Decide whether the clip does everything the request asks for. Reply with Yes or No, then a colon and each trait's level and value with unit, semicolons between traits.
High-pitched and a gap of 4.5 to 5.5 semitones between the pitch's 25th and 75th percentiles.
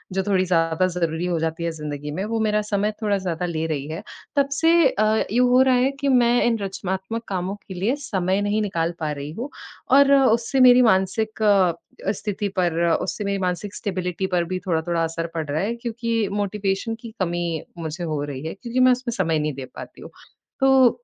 Yes: high, 195 Hz; average, 5.2 semitones